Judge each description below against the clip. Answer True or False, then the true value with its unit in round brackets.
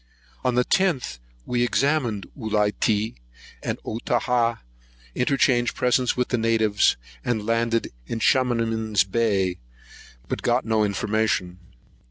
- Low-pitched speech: True (115 Hz)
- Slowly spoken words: True (110 wpm)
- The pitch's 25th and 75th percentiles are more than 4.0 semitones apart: False (2.5 semitones)